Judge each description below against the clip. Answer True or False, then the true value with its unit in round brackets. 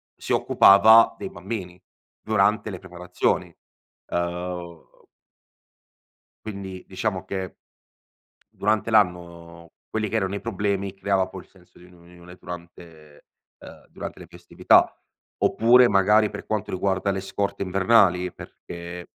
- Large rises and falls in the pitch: False (2.8 semitones)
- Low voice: True (95 Hz)